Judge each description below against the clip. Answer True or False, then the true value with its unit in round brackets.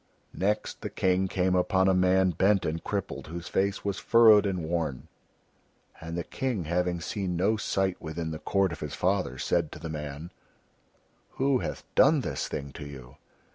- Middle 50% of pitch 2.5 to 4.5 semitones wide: True (3.4 semitones)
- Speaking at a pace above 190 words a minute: False (180 wpm)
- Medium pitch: False (90 Hz)